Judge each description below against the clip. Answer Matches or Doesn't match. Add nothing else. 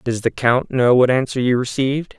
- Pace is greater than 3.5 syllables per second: Matches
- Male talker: Matches